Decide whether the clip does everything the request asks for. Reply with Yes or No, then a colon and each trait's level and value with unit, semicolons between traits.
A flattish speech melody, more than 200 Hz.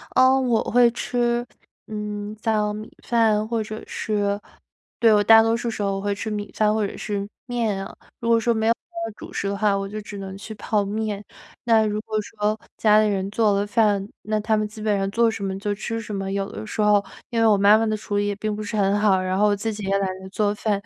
Yes: narrow, 1.6 semitones; high, 210 Hz